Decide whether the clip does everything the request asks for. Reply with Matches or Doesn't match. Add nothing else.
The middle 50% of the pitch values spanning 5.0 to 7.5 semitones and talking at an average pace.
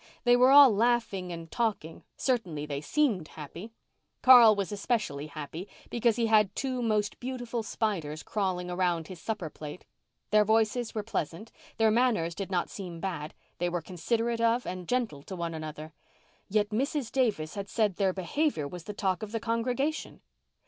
Matches